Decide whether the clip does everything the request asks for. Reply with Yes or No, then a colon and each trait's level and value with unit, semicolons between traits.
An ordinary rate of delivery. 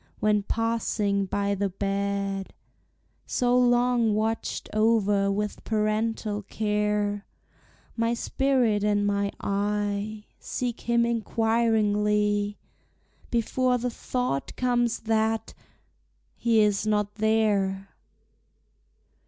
No: slow, 90 wpm